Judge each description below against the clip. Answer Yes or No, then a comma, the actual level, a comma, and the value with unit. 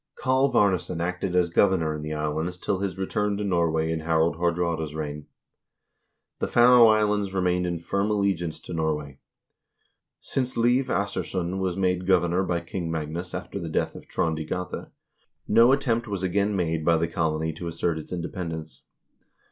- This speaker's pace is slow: No, average, 165 wpm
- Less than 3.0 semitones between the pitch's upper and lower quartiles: No, average, 3.5 semitones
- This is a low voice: Yes, very low, 90 Hz